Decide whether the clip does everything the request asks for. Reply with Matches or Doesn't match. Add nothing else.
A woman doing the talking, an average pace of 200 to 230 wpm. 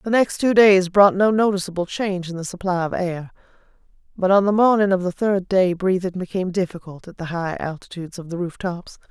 Matches